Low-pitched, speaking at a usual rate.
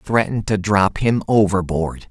Yes: low, 100 Hz; average, 145 wpm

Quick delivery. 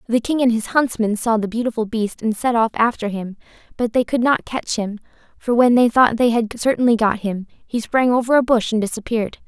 Yes: fast, 230 wpm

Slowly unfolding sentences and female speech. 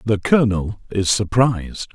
No: slow, 125 wpm; male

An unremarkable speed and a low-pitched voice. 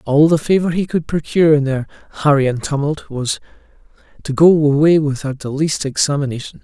No: average, 170 wpm; medium, 150 Hz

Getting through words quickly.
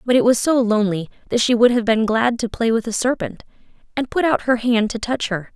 Yes: fast, 260 wpm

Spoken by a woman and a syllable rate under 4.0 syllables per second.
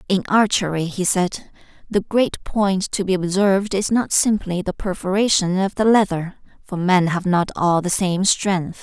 No: female; 4.4 syllables/s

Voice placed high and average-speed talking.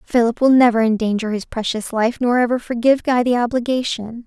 Yes: high, 235 Hz; average, 185 wpm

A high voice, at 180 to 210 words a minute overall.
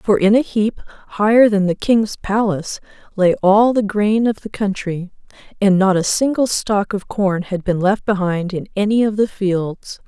Yes: high, 200 Hz; average, 190 wpm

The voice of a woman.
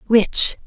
Yes: female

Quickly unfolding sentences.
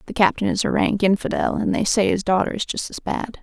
Yes: fast, 265 wpm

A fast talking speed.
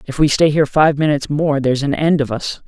Yes: fast, 270 wpm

